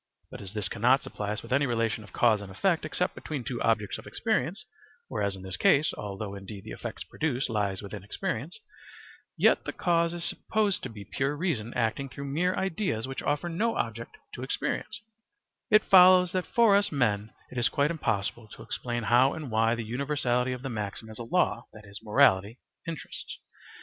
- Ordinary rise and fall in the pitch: No, wide, 6.5 semitones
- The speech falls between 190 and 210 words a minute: Yes, average, 195 wpm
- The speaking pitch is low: Yes, low, 120 Hz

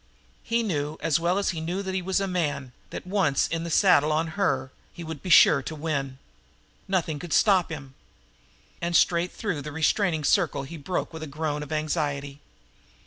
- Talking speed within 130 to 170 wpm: No, average, 195 wpm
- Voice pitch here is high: No, medium, 160 Hz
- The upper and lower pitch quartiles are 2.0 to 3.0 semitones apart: No, average, 3.7 semitones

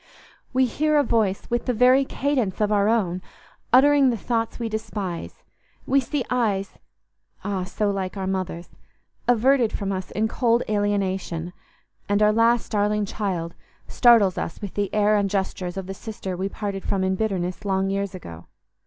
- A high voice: Yes, high, 205 Hz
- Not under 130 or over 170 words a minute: Yes, average, 160 wpm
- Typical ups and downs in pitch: Yes, average, 3.4 semitones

